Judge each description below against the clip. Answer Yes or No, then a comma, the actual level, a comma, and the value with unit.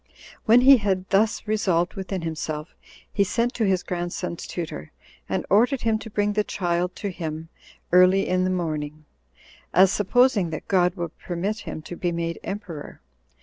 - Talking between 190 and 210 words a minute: No, average, 165 wpm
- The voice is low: No, medium, 185 Hz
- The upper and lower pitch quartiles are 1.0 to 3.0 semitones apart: No, average, 3.4 semitones